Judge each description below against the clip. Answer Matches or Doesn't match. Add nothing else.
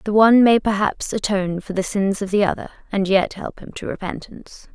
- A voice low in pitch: Doesn't match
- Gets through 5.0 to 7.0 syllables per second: Matches